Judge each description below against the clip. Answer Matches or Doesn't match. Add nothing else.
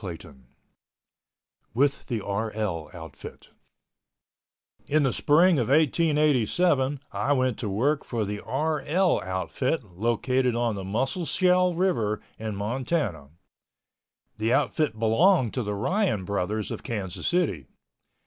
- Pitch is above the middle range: Doesn't match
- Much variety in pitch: Matches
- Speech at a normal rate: Doesn't match